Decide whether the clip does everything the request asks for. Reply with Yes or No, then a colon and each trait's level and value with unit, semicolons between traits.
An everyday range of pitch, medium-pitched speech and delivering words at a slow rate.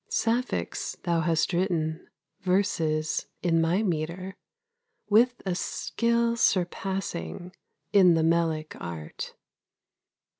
Yes: average, 3.4 semitones; medium, 175 Hz; slow, 90 wpm